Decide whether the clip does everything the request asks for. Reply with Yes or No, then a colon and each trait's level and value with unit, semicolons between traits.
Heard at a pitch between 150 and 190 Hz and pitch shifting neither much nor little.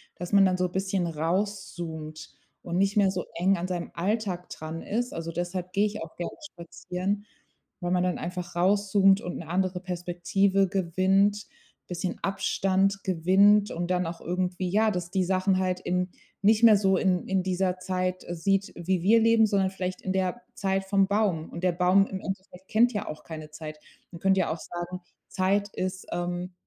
No: medium, 185 Hz; narrow, 1.9 semitones